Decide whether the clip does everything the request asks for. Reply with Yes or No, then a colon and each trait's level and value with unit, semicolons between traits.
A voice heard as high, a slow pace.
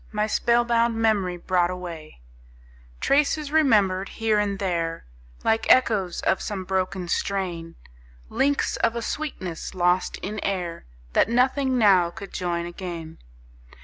Yes: high, 195 Hz; slow, 130 wpm